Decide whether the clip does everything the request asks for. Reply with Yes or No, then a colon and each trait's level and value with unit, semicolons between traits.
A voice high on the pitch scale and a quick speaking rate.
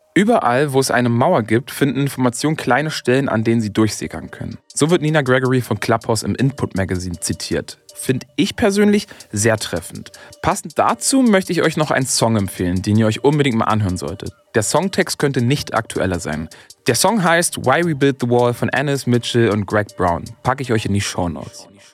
No: low, 125 Hz; fast, 200 wpm